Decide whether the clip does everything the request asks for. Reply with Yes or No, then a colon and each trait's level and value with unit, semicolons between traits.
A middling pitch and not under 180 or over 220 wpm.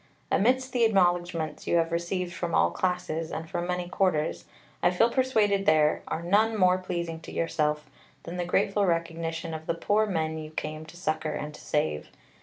Yes: medium, 170 Hz; average, 185 wpm